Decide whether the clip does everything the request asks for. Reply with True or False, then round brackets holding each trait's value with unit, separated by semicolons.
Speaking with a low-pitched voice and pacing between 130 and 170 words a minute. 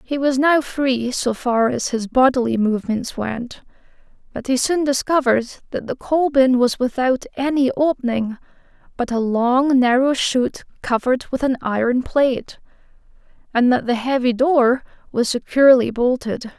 False (255 Hz; 150 wpm)